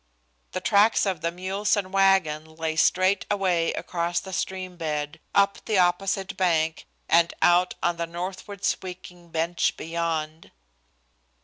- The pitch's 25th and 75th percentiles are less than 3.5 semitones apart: Yes, narrow, 2.5 semitones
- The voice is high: No, medium, 175 Hz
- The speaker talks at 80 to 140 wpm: Yes, slow, 135 wpm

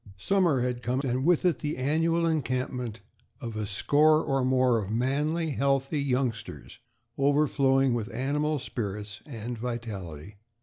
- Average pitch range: Yes, average, 4.0 semitones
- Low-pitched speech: Yes, low, 130 Hz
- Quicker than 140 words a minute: No, slow, 135 wpm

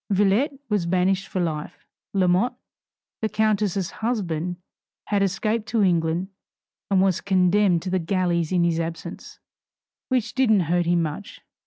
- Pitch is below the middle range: No, medium, 185 Hz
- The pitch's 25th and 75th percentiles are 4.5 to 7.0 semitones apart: No, average, 3.4 semitones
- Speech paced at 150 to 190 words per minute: No, average, 140 wpm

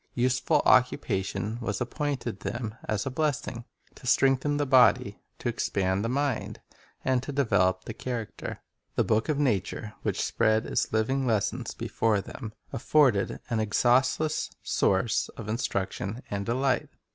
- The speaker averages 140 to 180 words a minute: Yes, average, 145 wpm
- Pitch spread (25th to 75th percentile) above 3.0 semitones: Yes, average, 3.7 semitones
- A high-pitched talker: No, low, 120 Hz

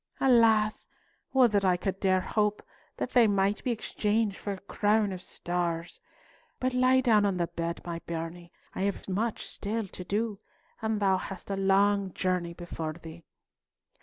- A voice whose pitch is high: Yes, high, 200 Hz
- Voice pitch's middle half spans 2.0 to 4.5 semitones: Yes, average, 3.4 semitones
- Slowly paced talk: No, average, 165 wpm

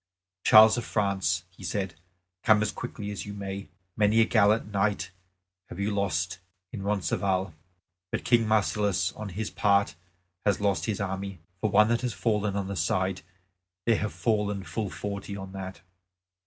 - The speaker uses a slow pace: No, average, 165 wpm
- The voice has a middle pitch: No, low, 100 Hz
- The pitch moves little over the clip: Yes, narrow, 1.7 semitones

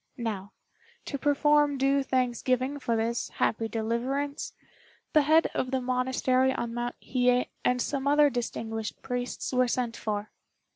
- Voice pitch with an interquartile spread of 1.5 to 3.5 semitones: Yes, average, 2.8 semitones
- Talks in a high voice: Yes, very high, 255 Hz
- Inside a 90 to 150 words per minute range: Yes, average, 140 wpm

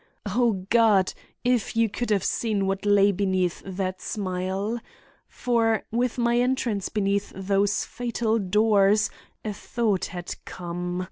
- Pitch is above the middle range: Yes, high, 205 Hz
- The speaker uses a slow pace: Yes, slow, 130 wpm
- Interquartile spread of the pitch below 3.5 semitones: Yes, average, 3.1 semitones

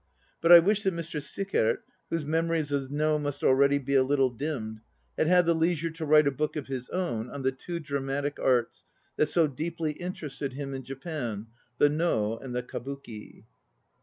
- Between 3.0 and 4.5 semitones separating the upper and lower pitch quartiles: Yes, average, 3.6 semitones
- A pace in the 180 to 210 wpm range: Yes, average, 190 wpm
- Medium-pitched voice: Yes, medium, 145 Hz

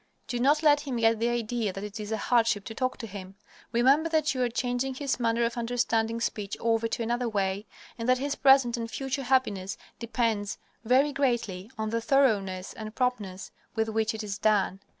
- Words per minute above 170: Yes, average, 200 wpm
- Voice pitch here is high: Yes, high, 230 Hz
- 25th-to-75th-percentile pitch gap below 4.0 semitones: Yes, average, 3.0 semitones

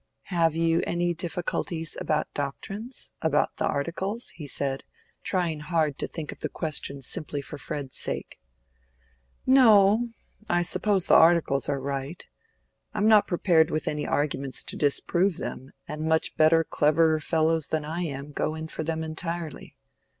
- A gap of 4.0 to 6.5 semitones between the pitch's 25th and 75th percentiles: No, average, 2.7 semitones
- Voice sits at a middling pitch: Yes, medium, 160 Hz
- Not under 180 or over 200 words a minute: No, average, 150 wpm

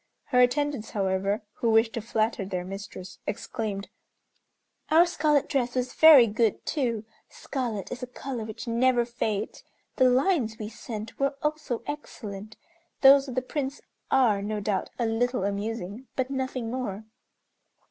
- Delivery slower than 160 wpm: Yes, average, 145 wpm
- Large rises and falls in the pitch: No, average, 3.8 semitones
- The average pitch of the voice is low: No, high, 235 Hz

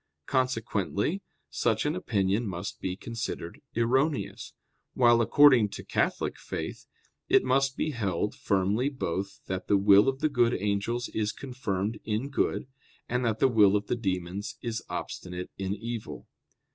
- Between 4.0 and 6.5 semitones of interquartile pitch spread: Yes, average, 4.4 semitones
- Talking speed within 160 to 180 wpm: No, average, 145 wpm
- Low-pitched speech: Yes, low, 110 Hz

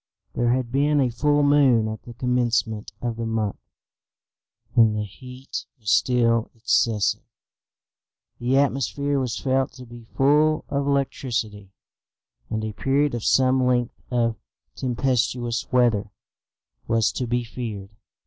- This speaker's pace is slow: Yes, slow, 130 wpm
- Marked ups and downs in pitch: No, average, 2.8 semitones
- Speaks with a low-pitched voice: Yes, low, 120 Hz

